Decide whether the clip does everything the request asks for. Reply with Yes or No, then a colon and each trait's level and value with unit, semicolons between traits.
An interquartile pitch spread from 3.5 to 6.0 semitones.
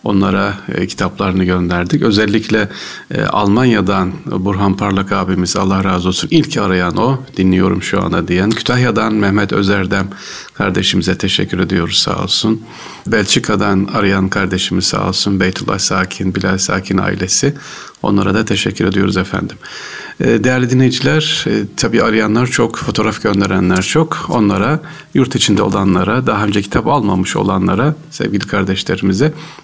No: average, 3.1 semitones